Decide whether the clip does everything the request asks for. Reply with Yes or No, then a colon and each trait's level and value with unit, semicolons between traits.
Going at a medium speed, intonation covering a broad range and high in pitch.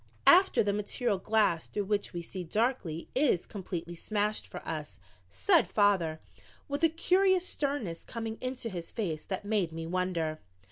Yes: average, 155 wpm; wide, 6.5 semitones; high, 205 Hz